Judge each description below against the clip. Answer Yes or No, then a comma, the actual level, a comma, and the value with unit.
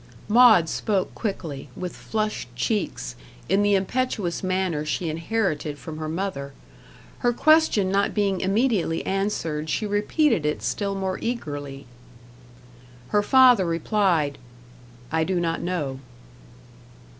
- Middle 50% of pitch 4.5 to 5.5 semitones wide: Yes, average, 5.1 semitones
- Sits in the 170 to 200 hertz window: Yes, medium, 185 Hz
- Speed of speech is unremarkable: No, slow, 120 wpm